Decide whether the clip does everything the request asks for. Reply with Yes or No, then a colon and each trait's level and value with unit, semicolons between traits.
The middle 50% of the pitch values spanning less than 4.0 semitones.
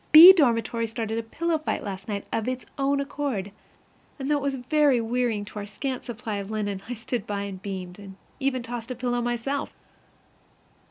No: average, 4.7 semitones